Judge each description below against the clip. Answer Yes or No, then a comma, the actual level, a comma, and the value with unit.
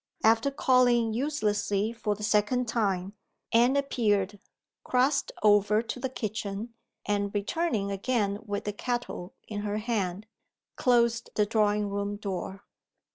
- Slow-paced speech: Yes, slow, 130 wpm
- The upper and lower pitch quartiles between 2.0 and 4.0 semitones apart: Yes, average, 2.9 semitones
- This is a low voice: No, high, 215 Hz